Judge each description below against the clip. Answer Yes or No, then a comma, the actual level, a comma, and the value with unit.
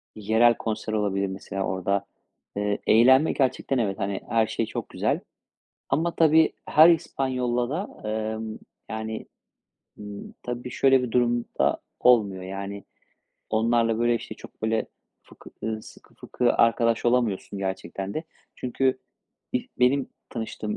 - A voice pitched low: Yes, low, 115 Hz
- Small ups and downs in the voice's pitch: No, average, 3.3 semitones